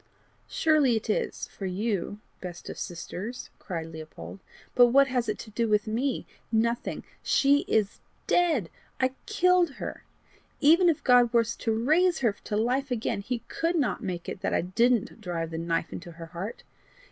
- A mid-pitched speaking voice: No, high, 230 Hz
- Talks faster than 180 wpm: No, average, 170 wpm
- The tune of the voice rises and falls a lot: Yes, wide, 6.0 semitones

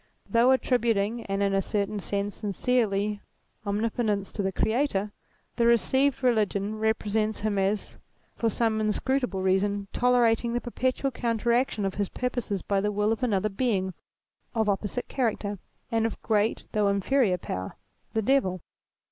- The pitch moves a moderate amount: Yes, average, 3.0 semitones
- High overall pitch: Yes, high, 215 Hz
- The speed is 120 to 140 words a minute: No, average, 150 wpm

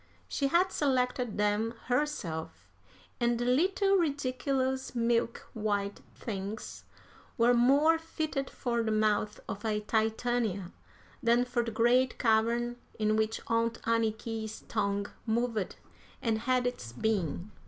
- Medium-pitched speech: No, high, 230 Hz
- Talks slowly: Yes, slow, 120 wpm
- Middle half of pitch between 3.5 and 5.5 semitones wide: No, average, 2.8 semitones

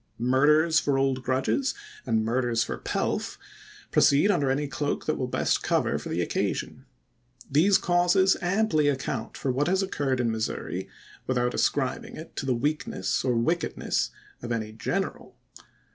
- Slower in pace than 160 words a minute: Yes, average, 150 wpm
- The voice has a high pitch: No, low, 135 Hz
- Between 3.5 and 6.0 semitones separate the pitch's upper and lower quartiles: Yes, average, 4.3 semitones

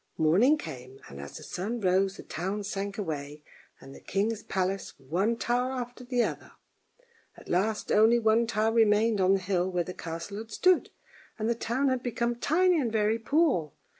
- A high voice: Yes, high, 210 Hz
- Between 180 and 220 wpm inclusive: Yes, average, 185 wpm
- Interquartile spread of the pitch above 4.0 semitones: Yes, average, 4.5 semitones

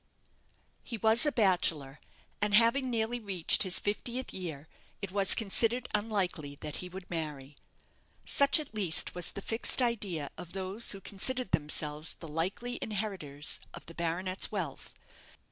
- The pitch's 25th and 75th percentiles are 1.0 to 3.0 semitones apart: No, wide, 5.5 semitones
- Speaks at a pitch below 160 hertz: No, high, 190 Hz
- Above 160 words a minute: No, average, 145 wpm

